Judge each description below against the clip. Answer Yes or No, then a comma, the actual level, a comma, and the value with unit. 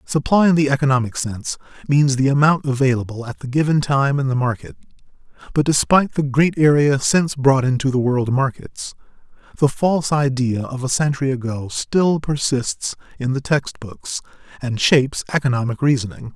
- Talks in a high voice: No, low, 135 Hz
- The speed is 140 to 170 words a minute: Yes, average, 160 wpm